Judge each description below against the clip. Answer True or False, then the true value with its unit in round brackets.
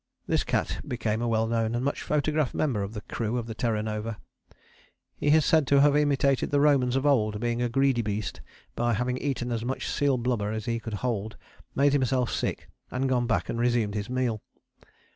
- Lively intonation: False (3.4 semitones)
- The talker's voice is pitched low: True (120 Hz)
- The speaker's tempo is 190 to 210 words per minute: True (205 wpm)